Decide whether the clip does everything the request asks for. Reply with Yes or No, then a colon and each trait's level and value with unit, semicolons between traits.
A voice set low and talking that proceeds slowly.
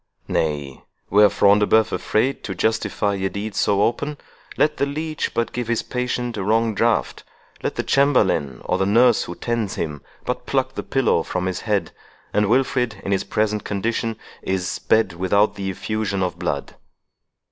No: low, 105 Hz; average, 170 wpm